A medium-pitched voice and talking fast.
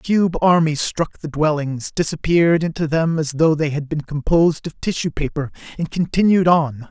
No: medium, 160 Hz; average, 185 wpm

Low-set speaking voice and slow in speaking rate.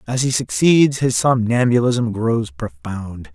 Yes: low, 115 Hz; slow, 125 wpm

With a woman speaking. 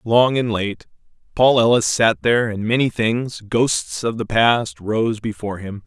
No: male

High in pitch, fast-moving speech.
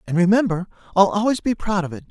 Yes: high, 195 Hz; fast, 230 wpm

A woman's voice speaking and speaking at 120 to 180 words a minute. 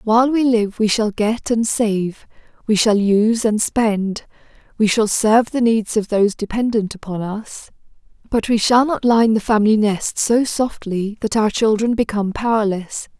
Yes: female; average, 175 wpm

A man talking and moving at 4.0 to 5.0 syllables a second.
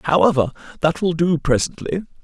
Yes: male; 4.7 syllables/s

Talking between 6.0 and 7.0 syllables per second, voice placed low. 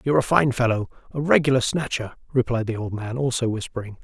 Yes: 6.2 syllables/s; low, 120 Hz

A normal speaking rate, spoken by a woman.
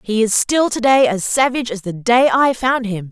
No: fast, 230 wpm; female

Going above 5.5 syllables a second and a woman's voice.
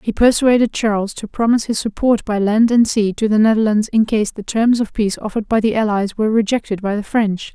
Yes: 5.9 syllables/s; female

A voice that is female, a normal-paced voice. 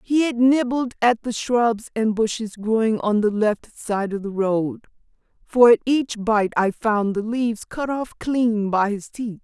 Yes: female; average, 190 wpm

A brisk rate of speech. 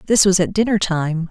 Yes: fast, 230 wpm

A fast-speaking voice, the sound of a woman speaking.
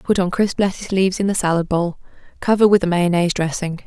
Yes: fast, 215 wpm; female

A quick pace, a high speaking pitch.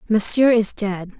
No: average, 150 wpm; high, 210 Hz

